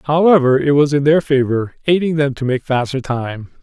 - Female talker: No, male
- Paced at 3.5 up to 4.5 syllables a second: No, 5.2 syllables/s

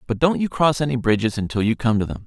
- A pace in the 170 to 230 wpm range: No, fast, 290 wpm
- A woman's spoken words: No, male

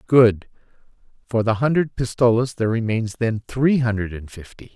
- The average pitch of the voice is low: Yes, low, 115 Hz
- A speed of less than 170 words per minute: Yes, average, 150 wpm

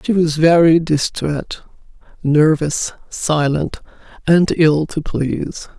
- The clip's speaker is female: Yes, female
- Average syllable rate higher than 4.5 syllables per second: No, 3.7 syllables/s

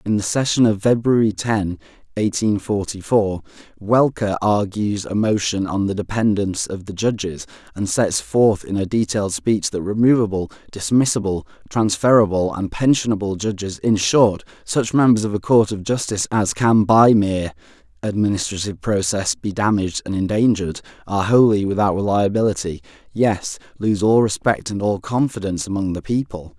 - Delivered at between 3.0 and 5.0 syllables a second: No, 5.2 syllables/s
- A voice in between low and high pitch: No, low, 105 Hz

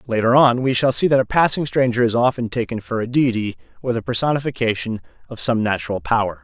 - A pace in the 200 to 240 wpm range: Yes, fast, 205 wpm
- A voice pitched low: Yes, low, 115 Hz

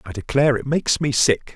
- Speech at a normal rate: No, fast, 230 wpm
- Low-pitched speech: Yes, low, 130 Hz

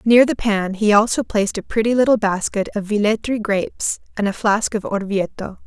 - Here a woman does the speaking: Yes, female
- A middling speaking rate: Yes, average, 190 wpm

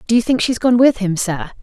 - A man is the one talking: No, female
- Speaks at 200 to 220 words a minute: No, fast, 295 wpm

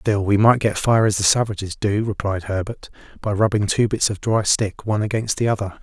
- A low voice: Yes, low, 105 Hz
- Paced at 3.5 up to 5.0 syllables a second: No, 5.5 syllables/s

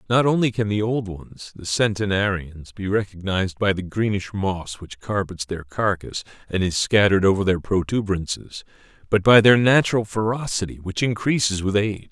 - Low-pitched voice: Yes, low, 100 Hz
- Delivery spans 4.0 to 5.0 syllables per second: No, 5.2 syllables/s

